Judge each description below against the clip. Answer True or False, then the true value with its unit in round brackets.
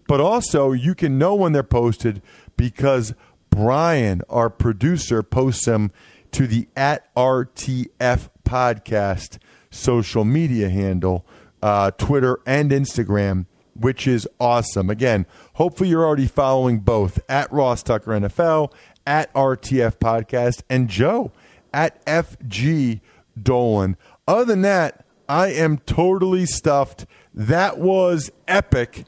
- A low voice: True (125 Hz)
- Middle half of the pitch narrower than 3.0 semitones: False (5.1 semitones)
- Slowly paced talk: True (120 wpm)